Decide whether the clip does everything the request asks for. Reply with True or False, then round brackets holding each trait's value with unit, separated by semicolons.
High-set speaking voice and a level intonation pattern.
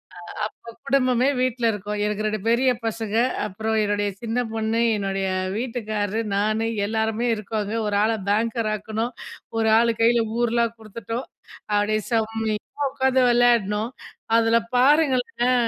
True (225 Hz; 2.0 semitones)